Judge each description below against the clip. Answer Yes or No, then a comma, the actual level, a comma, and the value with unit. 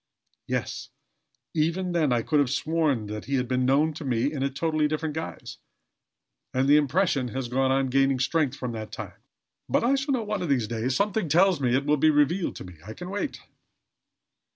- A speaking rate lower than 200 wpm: No, fast, 205 wpm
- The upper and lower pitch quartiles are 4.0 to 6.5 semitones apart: Yes, average, 4.3 semitones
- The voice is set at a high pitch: No, medium, 145 Hz